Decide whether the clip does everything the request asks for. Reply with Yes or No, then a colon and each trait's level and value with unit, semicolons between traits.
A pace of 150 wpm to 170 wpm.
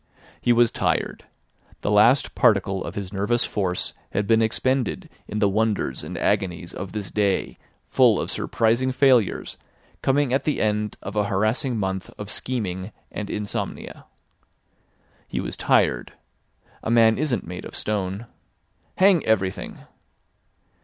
No: average, 140 wpm